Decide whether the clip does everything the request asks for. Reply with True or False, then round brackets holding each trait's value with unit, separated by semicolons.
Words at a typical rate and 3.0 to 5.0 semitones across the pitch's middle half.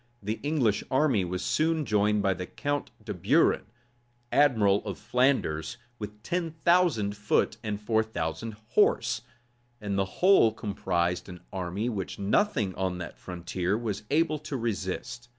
False (145 wpm; 5.5 semitones)